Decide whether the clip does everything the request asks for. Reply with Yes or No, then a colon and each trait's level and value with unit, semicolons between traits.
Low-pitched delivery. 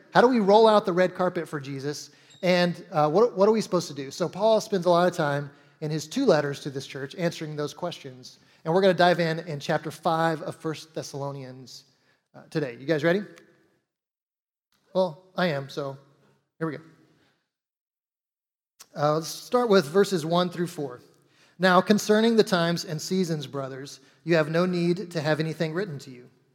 No: medium, 160 Hz